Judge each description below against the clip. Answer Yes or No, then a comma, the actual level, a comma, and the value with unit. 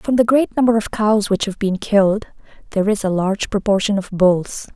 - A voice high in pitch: Yes, high, 205 Hz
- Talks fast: Yes, fast, 215 wpm